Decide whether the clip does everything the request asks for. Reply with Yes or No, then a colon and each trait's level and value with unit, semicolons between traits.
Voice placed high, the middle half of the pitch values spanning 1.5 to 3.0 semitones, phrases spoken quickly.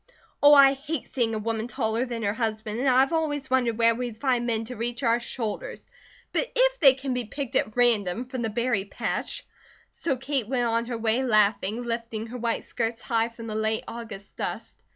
Yes: high, 235 Hz; narrow, 2.6 semitones; fast, 210 wpm